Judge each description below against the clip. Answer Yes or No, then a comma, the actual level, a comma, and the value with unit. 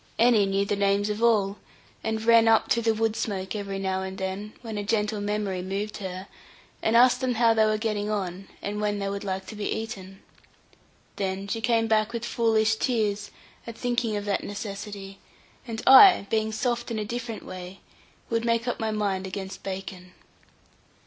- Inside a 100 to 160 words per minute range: No, average, 190 wpm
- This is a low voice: No, high, 210 Hz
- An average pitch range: No, narrow, 2.3 semitones